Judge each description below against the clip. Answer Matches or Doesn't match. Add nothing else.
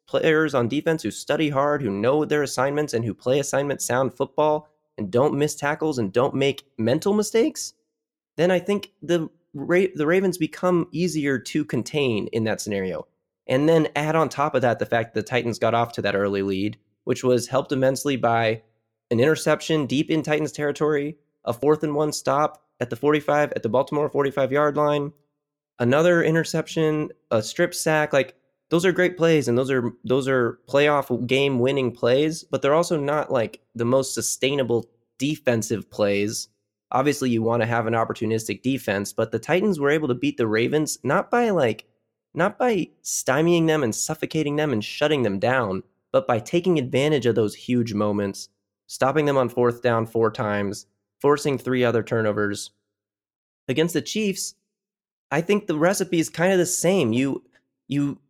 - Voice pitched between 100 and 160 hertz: Matches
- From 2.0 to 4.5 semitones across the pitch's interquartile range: Doesn't match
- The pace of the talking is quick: Doesn't match